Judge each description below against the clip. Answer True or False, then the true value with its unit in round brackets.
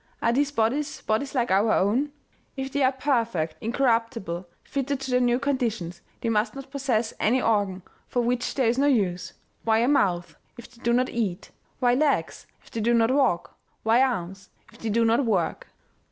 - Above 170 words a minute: True (190 wpm)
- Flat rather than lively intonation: False (3.9 semitones)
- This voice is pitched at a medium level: False (235 Hz)